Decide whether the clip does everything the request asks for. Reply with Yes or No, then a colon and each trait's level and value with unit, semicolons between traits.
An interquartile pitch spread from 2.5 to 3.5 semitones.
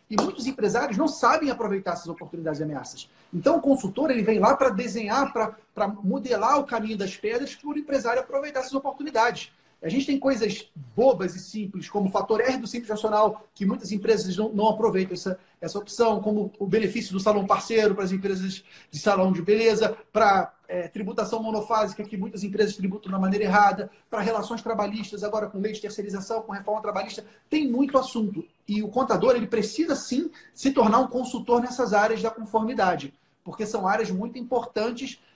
Yes: average, 2.9 semitones